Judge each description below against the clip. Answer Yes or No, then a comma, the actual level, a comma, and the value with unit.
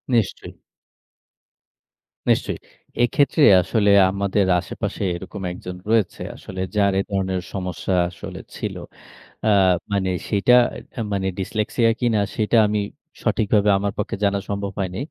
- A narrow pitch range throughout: Yes, narrow, 2.0 semitones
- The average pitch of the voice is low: Yes, low, 100 Hz